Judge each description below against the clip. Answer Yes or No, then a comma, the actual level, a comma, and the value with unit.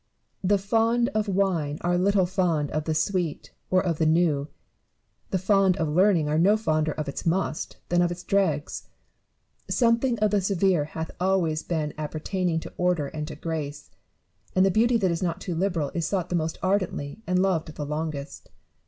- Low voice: No, medium, 175 Hz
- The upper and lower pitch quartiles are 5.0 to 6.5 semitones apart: No, average, 3.8 semitones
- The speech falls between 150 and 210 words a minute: Yes, average, 185 wpm